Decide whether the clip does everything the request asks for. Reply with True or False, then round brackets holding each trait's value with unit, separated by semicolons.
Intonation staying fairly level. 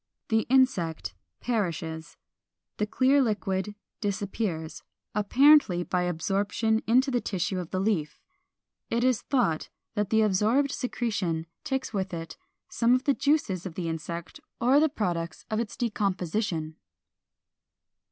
False (5.5 semitones)